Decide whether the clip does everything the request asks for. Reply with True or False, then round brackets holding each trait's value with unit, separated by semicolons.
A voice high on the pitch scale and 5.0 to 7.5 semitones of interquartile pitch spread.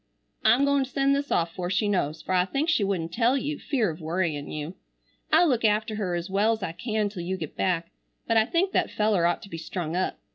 True (200 Hz; 5.5 semitones)